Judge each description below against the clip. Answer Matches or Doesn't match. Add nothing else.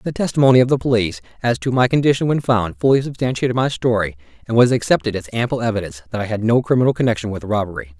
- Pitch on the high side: Doesn't match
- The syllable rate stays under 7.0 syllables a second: Doesn't match